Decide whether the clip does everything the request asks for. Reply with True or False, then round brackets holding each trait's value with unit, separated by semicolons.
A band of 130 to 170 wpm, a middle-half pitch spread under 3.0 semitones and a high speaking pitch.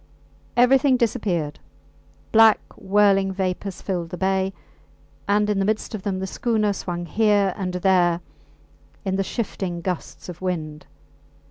True (135 wpm; 2.6 semitones; 195 Hz)